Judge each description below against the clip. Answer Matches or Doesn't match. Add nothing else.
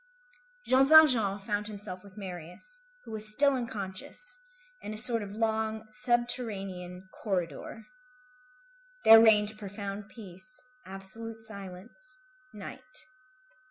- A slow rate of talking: Matches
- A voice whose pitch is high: Matches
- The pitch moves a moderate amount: Matches